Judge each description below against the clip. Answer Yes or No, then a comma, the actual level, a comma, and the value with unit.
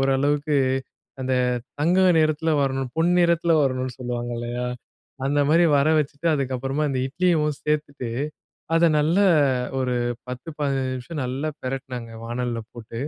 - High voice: No, low, 135 Hz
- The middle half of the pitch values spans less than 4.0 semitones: Yes, average, 3.3 semitones